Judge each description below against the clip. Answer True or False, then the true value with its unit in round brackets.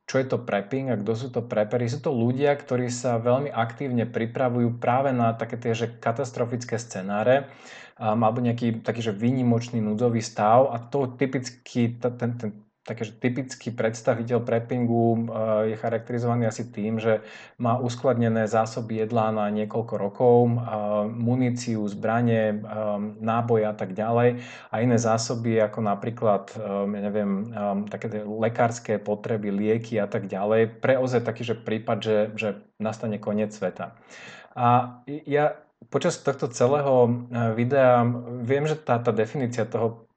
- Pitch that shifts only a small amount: True (2.0 semitones)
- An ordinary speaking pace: True (140 wpm)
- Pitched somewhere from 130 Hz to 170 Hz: False (115 Hz)